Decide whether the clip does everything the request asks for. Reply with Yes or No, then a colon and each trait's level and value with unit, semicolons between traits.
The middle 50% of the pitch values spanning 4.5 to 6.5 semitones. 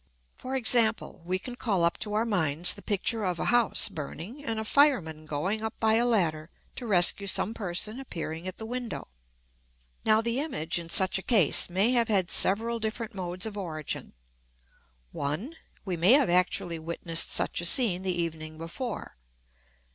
Yes: average, 5.2 semitones